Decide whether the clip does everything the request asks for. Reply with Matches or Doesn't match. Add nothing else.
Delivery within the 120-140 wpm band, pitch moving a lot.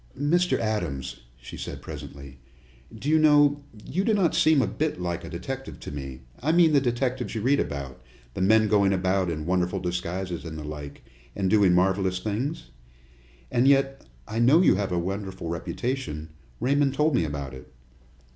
Doesn't match